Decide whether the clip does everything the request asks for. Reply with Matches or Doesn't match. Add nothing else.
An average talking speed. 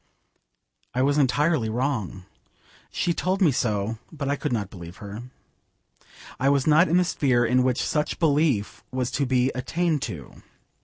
Matches